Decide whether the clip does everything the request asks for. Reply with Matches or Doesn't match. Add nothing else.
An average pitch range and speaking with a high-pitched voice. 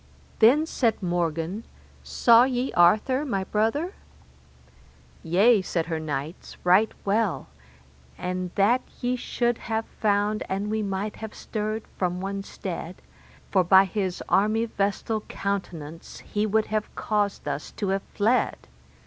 Matches